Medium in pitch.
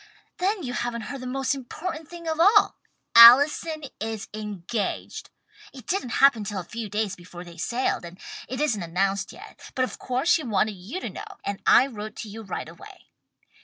No: high, 235 Hz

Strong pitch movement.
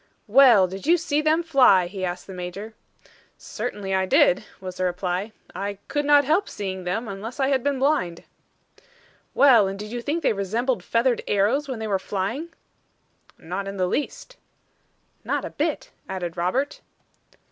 Yes: wide, 6.4 semitones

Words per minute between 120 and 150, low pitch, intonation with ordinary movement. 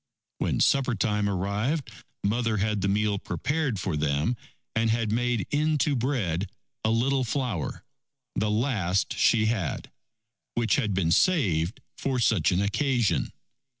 Yes: slow, 135 wpm; low, 110 Hz; average, 4.4 semitones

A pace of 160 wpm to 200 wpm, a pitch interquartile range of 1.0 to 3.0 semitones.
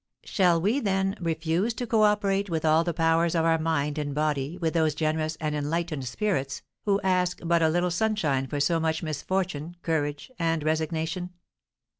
Yes: average, 170 wpm; average, 2.7 semitones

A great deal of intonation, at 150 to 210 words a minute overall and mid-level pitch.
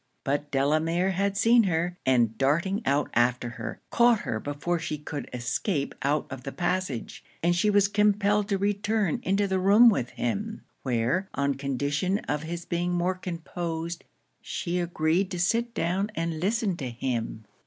Yes: wide, 5.8 semitones; average, 165 wpm; medium, 170 Hz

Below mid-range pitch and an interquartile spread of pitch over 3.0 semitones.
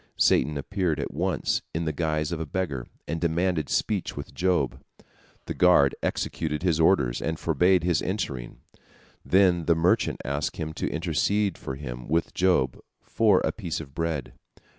Yes: very low, 80 Hz; average, 3.7 semitones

